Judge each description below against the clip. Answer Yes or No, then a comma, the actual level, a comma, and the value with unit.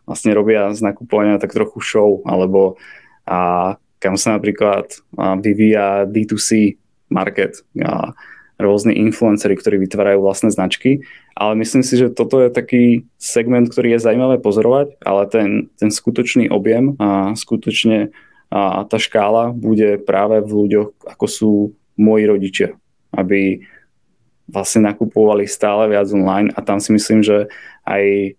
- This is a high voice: No, low, 105 Hz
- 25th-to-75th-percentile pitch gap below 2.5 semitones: Yes, narrow, 1.8 semitones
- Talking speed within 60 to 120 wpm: No, average, 140 wpm